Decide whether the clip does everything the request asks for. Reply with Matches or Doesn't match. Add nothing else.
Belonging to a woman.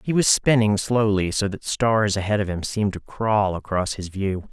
Doesn't match